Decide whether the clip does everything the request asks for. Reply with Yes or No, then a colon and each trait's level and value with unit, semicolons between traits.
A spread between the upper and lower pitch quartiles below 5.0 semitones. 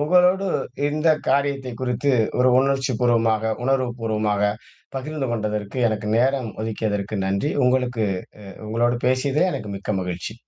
Yes: average, 3.9 semitones